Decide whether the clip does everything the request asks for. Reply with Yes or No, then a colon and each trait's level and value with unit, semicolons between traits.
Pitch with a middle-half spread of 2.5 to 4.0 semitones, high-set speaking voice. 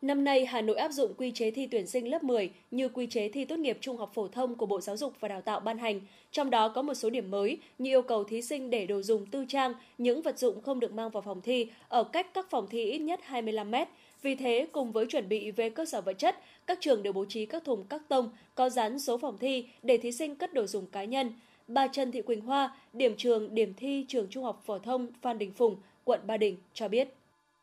Yes: average, 3.6 semitones; high, 245 Hz